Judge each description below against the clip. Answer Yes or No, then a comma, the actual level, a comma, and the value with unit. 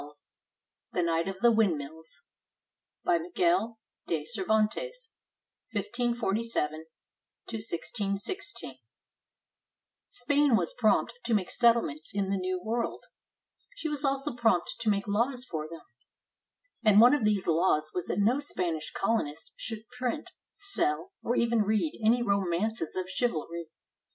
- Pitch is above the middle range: Yes, high, 220 Hz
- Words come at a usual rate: No, slow, 125 wpm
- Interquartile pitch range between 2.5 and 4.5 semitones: No, wide, 5.4 semitones